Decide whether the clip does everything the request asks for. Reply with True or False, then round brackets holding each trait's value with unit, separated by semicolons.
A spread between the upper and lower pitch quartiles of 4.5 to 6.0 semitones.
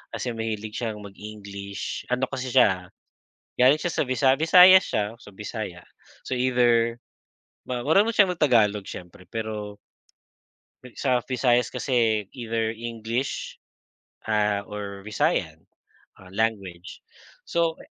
False (3.5 semitones)